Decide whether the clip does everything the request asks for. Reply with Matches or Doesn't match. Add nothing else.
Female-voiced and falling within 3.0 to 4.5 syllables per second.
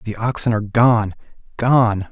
Doesn't match